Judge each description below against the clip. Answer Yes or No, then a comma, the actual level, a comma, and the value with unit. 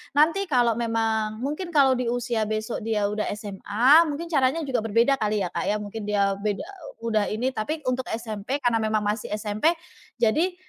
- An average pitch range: Yes, average, 4.1 semitones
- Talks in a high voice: Yes, high, 230 Hz